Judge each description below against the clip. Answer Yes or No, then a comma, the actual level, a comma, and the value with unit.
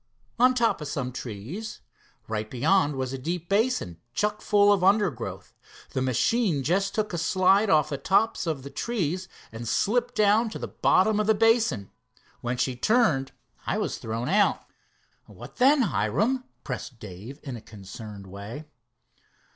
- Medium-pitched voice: Yes, medium, 170 Hz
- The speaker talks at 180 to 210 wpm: No, average, 160 wpm